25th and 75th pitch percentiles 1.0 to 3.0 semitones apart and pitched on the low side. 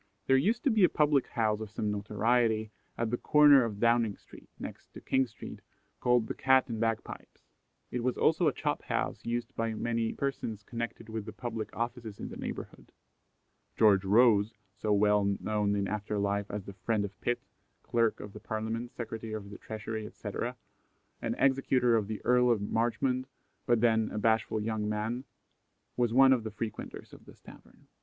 Yes: narrow, 2.4 semitones; low, 115 Hz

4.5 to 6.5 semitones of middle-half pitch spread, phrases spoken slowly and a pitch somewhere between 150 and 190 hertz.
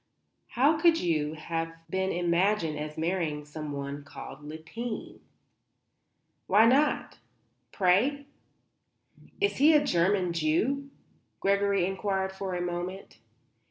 Yes: average, 5.0 semitones; slow, 105 wpm; medium, 185 Hz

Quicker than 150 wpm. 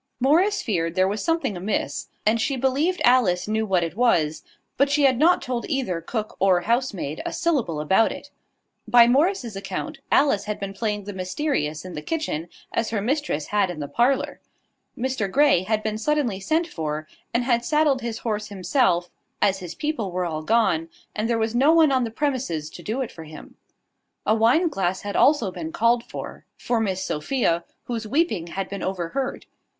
Yes: average, 190 wpm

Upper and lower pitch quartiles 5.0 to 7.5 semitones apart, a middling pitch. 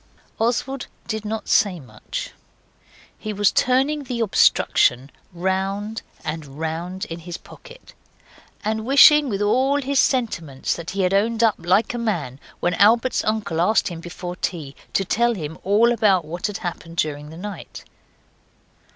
No: wide, 5.4 semitones; high, 200 Hz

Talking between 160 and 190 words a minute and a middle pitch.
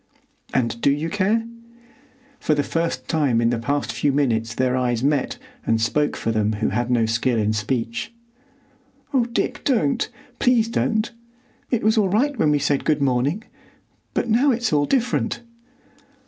Yes: average, 165 wpm; medium, 145 Hz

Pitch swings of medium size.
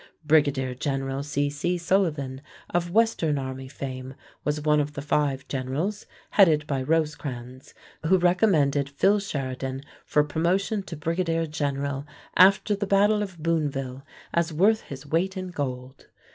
Yes: average, 4.5 semitones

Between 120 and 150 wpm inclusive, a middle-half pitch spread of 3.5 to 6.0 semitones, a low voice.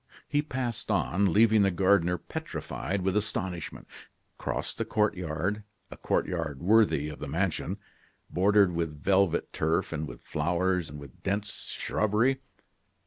Yes: average, 140 wpm; average, 4.1 semitones; very low, 95 Hz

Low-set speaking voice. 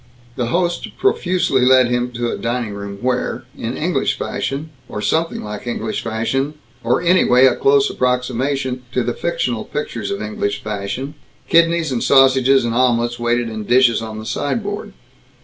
Yes: low, 125 Hz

